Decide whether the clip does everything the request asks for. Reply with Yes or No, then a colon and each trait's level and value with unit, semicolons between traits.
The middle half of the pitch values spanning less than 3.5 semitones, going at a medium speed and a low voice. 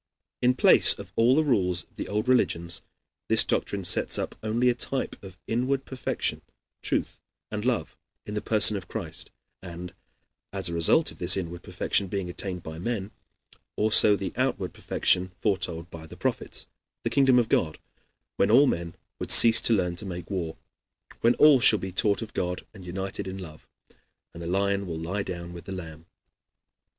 No: average, 4.4 semitones; average, 180 wpm; very low, 95 Hz